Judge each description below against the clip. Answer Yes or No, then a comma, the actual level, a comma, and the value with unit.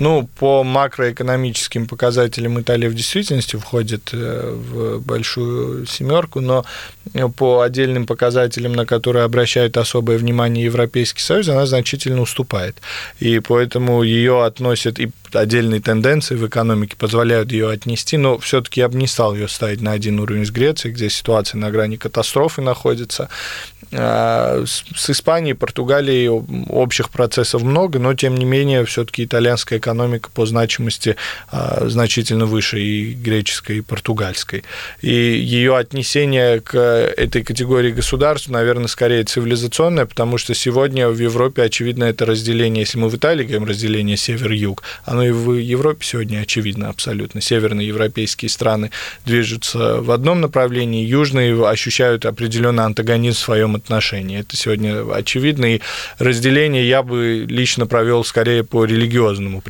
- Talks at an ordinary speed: Yes, average, 140 wpm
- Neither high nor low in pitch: No, low, 120 Hz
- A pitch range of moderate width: No, narrow, 2.1 semitones